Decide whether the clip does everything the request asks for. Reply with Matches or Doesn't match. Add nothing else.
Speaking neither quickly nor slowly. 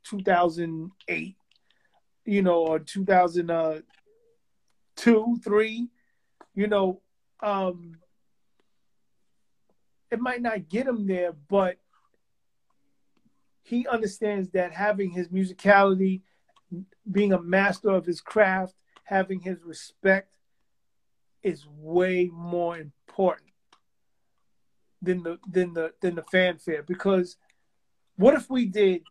Doesn't match